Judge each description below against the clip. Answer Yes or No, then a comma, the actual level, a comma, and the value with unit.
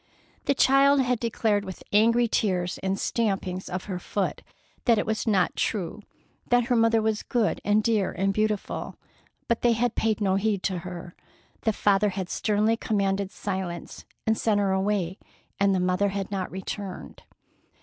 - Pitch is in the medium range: No, high, 205 Hz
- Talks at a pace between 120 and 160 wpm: No, average, 170 wpm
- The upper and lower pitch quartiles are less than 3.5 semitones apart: Yes, average, 2.7 semitones